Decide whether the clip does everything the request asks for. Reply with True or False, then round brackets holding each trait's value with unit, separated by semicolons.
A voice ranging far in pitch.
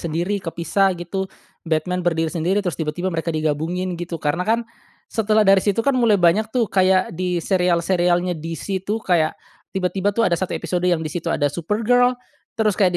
False (3.0 semitones)